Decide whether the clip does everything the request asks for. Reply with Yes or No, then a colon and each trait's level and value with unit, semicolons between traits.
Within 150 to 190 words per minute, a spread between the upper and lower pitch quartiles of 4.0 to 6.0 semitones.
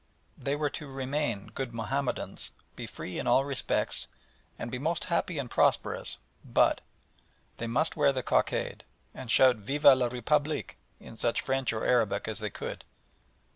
No: average, 160 wpm; average, 3.4 semitones